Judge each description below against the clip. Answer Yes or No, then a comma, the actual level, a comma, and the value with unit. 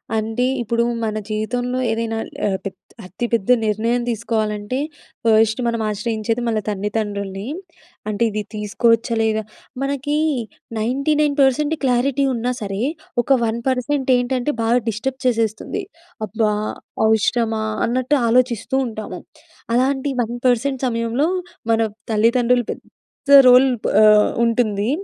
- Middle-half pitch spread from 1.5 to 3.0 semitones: Yes, average, 2.7 semitones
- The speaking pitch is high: Yes, high, 230 Hz